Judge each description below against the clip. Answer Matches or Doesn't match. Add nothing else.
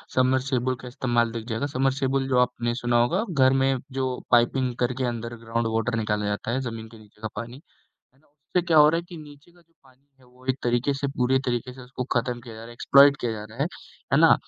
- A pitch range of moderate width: Doesn't match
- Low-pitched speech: Matches